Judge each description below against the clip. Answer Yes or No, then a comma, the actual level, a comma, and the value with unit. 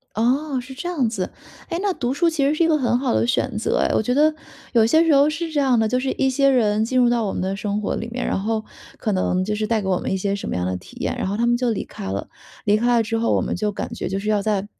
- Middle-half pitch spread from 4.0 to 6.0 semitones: Yes, average, 4.5 semitones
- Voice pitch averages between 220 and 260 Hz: Yes, high, 235 Hz